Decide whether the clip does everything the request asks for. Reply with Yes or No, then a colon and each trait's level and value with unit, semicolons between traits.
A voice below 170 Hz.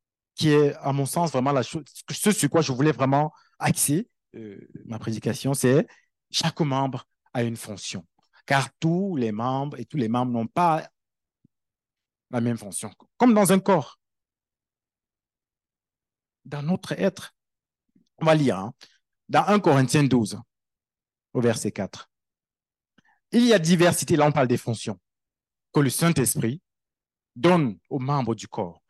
Yes: low, 135 Hz